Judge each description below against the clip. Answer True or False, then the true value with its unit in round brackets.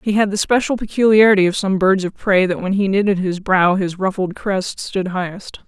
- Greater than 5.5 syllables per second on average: False (5.2 syllables/s)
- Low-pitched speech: False (195 Hz)